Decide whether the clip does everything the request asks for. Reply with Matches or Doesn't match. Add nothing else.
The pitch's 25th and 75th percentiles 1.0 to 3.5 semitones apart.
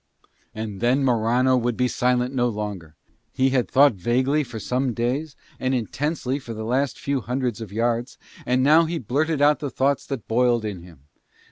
Matches